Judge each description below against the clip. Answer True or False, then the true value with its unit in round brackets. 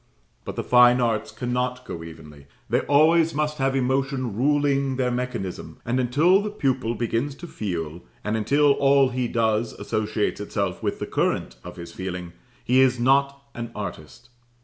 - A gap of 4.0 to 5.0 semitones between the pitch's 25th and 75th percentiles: True (4.4 semitones)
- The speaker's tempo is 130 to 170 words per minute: True (165 wpm)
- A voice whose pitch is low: True (125 Hz)